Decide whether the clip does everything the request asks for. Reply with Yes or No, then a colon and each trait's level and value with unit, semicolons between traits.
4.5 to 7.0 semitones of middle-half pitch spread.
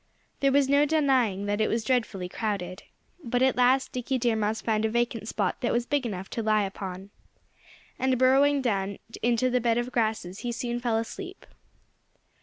No: average, 3.3 semitones